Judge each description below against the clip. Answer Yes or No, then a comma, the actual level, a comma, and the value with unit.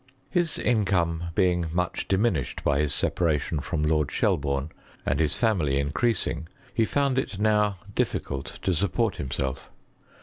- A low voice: Yes, very low, 85 Hz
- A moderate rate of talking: Yes, average, 145 wpm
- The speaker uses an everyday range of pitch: No, wide, 6.3 semitones